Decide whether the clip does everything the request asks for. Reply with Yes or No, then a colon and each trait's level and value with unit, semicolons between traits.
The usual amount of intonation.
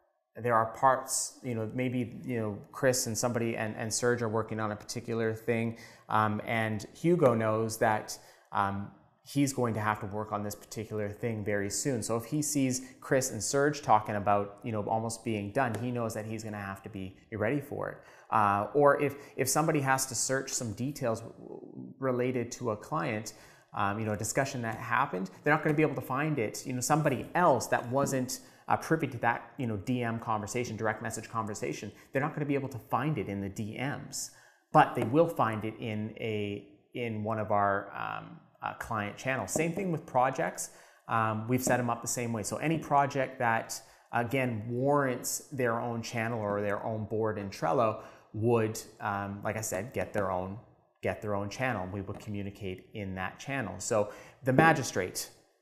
Yes: average, 3.5 semitones